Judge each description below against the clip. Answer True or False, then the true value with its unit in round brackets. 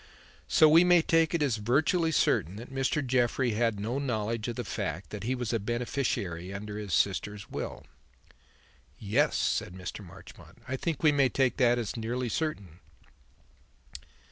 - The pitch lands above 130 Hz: False (120 Hz)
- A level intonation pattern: False (4.8 semitones)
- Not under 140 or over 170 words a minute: True (165 wpm)